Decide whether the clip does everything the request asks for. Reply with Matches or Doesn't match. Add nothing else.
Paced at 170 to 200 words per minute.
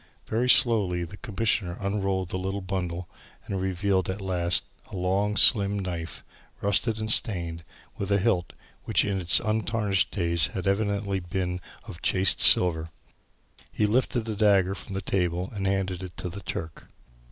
Doesn't match